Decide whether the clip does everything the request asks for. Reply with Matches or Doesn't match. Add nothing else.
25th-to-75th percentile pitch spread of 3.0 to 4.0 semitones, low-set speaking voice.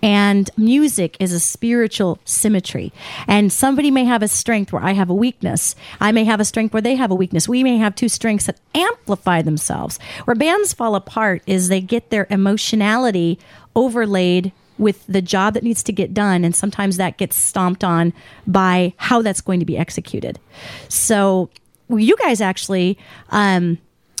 Doesn't match